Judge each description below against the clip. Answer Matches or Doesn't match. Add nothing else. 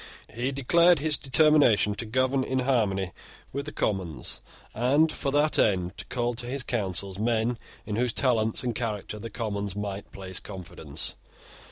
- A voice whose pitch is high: Doesn't match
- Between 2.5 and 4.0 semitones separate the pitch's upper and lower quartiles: Doesn't match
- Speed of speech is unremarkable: Matches